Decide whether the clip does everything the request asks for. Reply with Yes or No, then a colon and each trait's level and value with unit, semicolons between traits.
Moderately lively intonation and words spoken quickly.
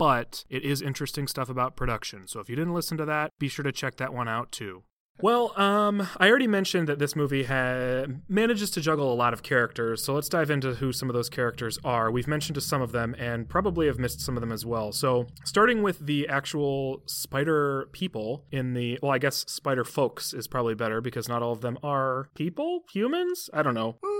Yes: average, 4.1 semitones; fast, 225 wpm